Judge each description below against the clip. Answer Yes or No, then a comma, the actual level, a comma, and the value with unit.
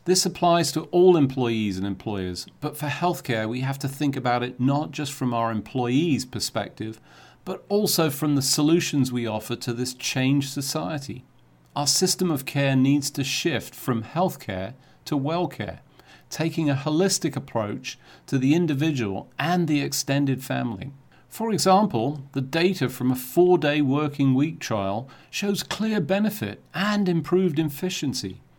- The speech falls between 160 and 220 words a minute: No, average, 150 wpm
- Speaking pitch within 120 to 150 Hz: Yes, medium, 140 Hz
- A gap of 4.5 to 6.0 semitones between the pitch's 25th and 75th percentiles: Yes, average, 4.8 semitones